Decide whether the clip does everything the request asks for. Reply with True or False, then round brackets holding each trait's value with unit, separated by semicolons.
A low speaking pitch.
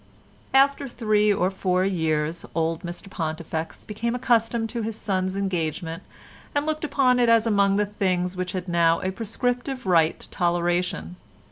False (190 Hz)